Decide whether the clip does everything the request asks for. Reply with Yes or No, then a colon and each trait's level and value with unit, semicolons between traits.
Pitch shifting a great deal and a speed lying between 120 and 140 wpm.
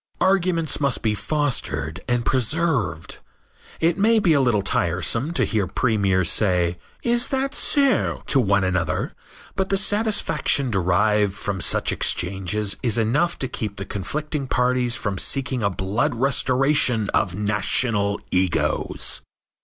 Yes: wide, 7.1 semitones; slow, 135 wpm